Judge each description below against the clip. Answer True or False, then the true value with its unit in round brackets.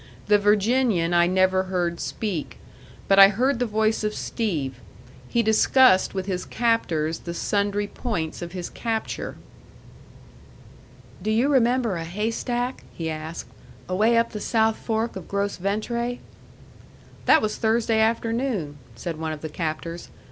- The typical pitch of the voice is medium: False (205 Hz)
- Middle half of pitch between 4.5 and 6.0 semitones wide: True (4.8 semitones)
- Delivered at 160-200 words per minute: False (140 wpm)